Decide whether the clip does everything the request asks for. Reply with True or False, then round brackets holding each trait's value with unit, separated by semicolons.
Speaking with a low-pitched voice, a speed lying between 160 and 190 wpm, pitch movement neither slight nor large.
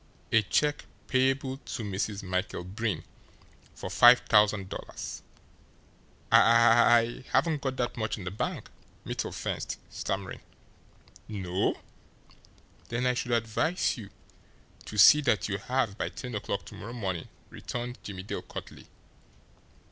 False (110 Hz; 135 wpm; 3.8 semitones)